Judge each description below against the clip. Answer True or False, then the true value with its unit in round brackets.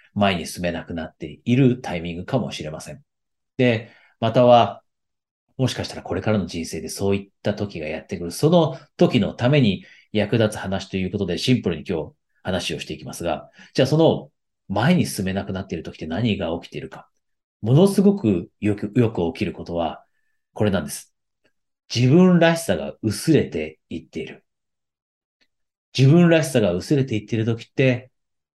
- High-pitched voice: False (115 Hz)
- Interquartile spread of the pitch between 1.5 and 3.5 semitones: False (5.6 semitones)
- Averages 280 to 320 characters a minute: False (345 characters per minute)